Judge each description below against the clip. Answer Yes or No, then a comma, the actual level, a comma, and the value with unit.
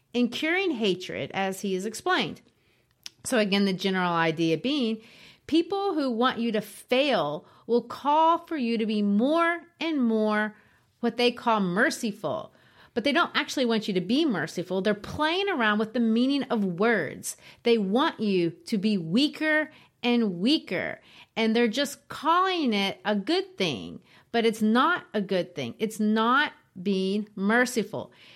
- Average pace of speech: Yes, average, 160 wpm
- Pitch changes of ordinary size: No, wide, 5.7 semitones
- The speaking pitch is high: Yes, high, 230 Hz